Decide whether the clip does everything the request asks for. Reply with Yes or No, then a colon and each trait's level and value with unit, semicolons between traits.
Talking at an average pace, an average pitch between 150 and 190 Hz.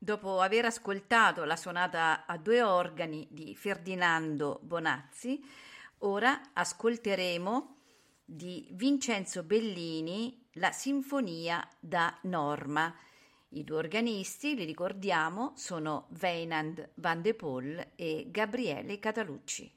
No: slow, 100 wpm; medium, 185 Hz